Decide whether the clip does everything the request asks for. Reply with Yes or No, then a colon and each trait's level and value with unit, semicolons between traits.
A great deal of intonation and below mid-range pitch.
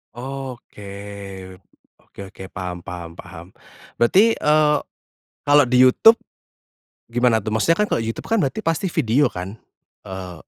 Yes: wide, 7.6 semitones; low, 120 Hz